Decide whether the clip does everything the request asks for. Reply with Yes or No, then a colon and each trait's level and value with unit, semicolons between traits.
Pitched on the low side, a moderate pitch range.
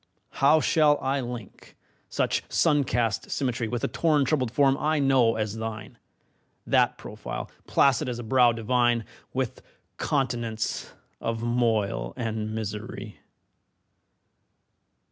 Yes: low, 120 Hz; average, 3.3 semitones